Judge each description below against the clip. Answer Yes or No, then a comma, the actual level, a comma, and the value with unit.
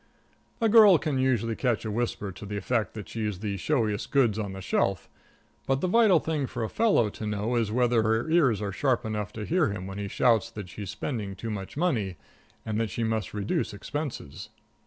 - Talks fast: Yes, fast, 210 wpm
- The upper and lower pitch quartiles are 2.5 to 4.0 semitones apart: No, average, 4.4 semitones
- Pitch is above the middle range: No, low, 110 Hz